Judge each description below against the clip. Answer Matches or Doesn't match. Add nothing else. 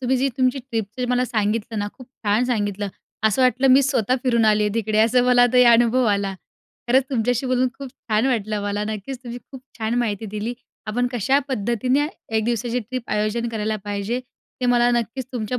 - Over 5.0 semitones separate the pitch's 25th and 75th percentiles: Doesn't match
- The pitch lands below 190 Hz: Doesn't match